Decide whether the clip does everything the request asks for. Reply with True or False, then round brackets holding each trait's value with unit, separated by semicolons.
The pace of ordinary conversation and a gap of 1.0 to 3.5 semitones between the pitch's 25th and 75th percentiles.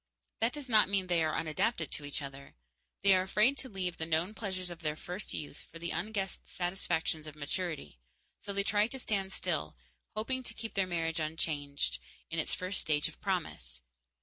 False (195 wpm; 4.4 semitones)